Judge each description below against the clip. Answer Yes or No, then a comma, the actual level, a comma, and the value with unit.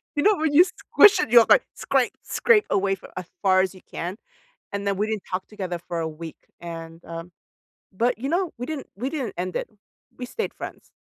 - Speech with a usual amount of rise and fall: No, wide, 7.8 semitones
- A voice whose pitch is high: Yes, high, 200 Hz